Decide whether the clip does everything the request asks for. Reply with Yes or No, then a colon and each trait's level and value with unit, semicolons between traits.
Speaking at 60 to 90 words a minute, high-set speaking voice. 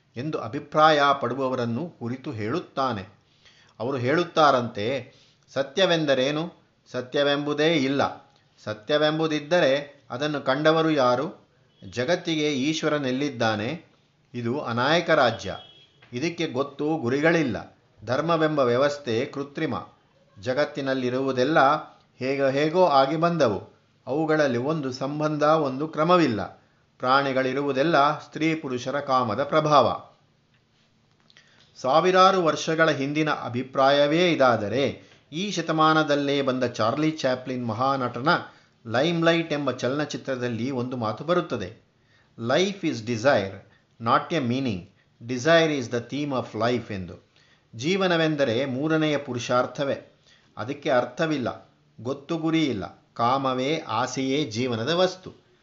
No: average, 85 wpm; medium, 140 Hz